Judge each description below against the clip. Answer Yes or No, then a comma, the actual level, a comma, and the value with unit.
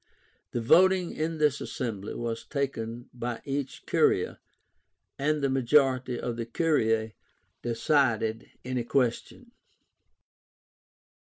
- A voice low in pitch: Yes, low, 130 Hz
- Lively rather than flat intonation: No, average, 4.1 semitones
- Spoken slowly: Yes, slow, 100 wpm